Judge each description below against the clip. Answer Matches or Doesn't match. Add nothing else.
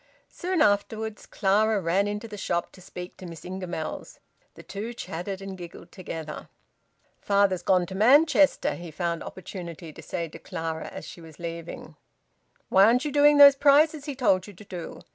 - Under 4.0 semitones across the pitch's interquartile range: Doesn't match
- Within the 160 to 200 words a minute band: Matches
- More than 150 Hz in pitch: Matches